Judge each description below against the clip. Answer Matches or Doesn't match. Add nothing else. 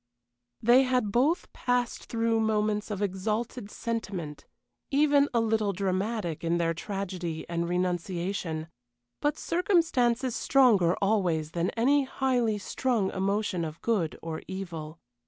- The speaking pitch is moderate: Doesn't match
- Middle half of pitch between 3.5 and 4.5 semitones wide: Doesn't match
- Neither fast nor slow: Doesn't match